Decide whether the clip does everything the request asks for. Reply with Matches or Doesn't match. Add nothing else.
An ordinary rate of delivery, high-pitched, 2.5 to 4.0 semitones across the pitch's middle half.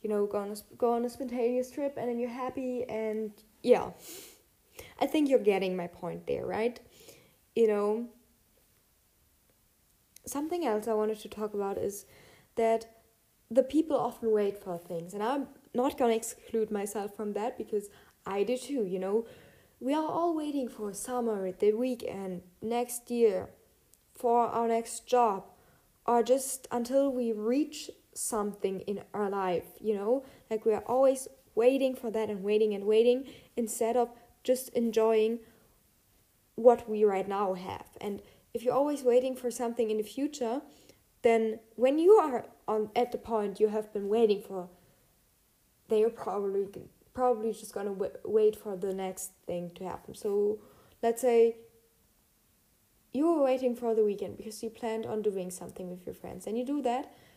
Matches